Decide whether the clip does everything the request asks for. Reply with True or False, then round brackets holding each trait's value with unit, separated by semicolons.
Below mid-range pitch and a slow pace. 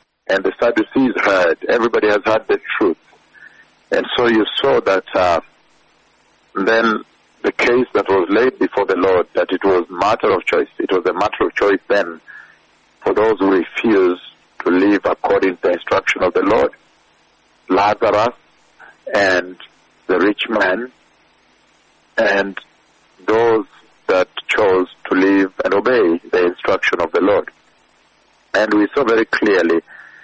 False (105 Hz; 145 wpm)